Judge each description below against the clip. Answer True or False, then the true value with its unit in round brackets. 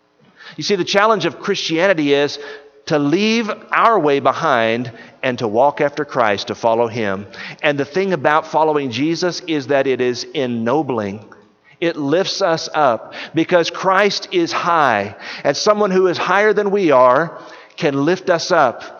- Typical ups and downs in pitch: False (5.8 semitones)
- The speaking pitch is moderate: True (150 Hz)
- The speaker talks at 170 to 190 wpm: False (160 wpm)